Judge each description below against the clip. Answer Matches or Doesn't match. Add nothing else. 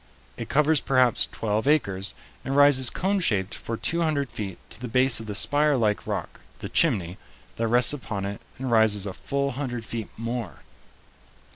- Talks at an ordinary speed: Matches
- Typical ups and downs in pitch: Matches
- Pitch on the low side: Matches